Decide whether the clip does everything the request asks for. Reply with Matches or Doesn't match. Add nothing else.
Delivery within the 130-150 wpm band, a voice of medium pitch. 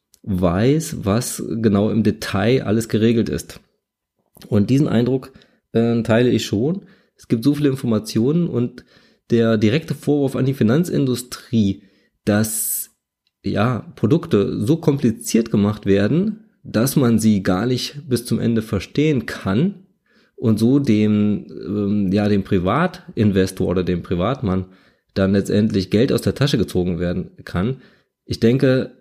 Doesn't match